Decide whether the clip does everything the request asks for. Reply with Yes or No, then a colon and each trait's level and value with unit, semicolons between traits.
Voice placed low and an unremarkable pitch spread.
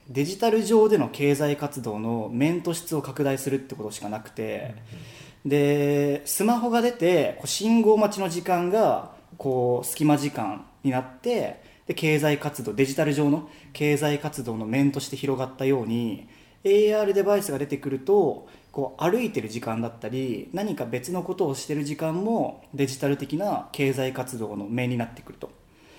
No: medium, 145 Hz; average, 4.2 semitones